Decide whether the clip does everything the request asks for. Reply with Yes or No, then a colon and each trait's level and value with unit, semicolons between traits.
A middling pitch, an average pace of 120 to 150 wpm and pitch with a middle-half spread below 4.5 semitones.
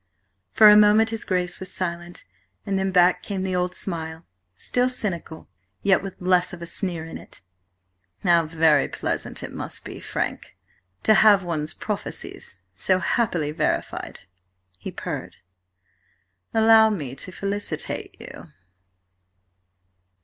Yes: medium, 180 Hz; slow, 135 wpm; average, 3.4 semitones